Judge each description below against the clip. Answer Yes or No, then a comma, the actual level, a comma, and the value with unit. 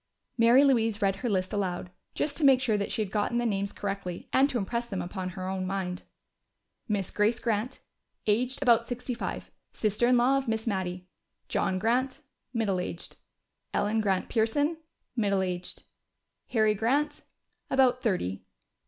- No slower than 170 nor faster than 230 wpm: No, average, 160 wpm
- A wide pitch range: No, average, 4.2 semitones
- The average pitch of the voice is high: Yes, high, 220 Hz